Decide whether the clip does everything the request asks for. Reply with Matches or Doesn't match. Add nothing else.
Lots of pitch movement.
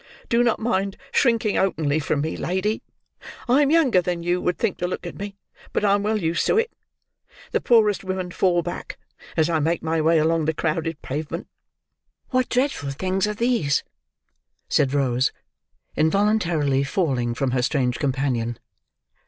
Matches